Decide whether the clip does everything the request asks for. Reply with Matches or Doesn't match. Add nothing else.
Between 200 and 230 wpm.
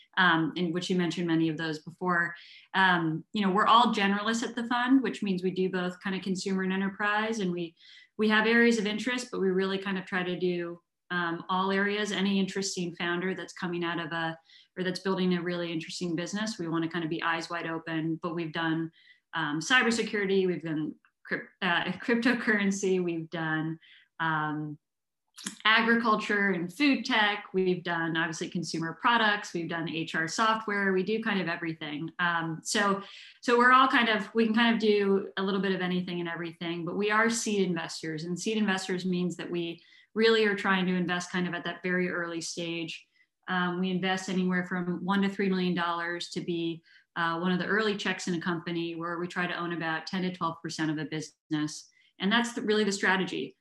Matches